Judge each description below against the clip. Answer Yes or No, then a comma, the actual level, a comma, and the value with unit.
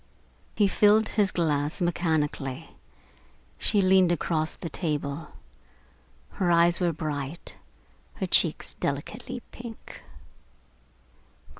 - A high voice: No, medium, 170 Hz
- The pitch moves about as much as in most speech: Yes, average, 3.9 semitones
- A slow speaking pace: Yes, slow, 95 wpm